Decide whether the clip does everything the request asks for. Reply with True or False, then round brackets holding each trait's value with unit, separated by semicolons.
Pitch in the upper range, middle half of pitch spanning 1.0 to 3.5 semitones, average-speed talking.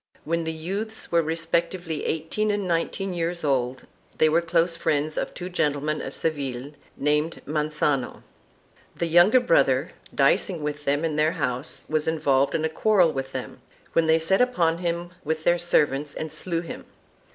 False (160 Hz; 2.6 semitones; 170 wpm)